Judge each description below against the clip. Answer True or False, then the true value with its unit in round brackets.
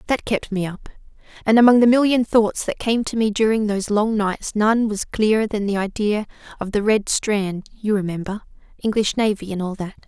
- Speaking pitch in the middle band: False (210 Hz)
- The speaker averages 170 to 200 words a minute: True (195 wpm)